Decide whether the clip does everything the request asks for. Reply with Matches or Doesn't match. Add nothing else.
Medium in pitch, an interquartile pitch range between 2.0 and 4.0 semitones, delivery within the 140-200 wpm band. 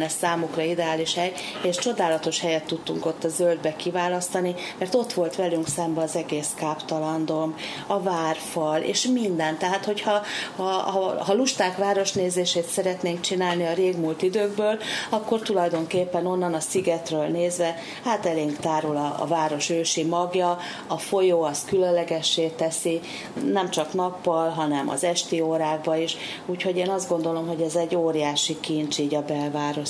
Matches